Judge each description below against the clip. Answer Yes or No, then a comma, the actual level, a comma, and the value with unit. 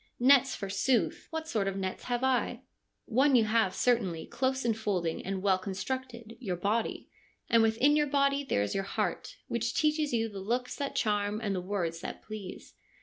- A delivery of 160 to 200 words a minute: Yes, average, 190 wpm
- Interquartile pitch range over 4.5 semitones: Yes, average, 5.0 semitones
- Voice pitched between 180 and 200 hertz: No, high, 225 Hz